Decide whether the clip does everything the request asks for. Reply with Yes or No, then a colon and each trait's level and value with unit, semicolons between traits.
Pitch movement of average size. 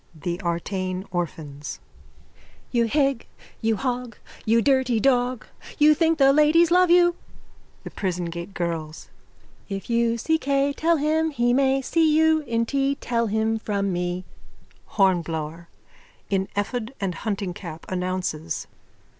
No: wide, 7.2 semitones